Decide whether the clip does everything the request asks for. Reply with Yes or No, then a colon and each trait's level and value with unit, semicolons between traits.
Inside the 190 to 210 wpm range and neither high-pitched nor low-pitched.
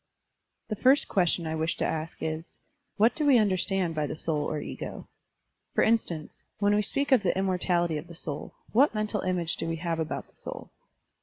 Yes: average, 200 wpm; medium, 180 Hz